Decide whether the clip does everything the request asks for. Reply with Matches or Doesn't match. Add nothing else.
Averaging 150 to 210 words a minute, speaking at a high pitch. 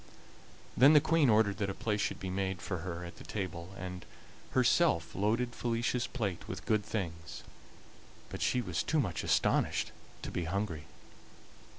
Doesn't match